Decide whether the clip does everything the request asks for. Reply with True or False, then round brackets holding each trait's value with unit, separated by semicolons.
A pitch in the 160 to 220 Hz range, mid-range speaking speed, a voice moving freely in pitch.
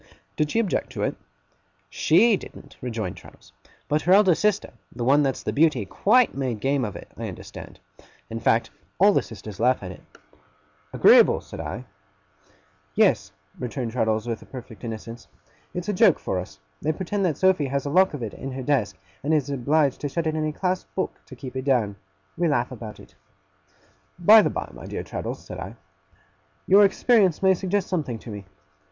False (140 Hz; 190 wpm; 7.2 semitones)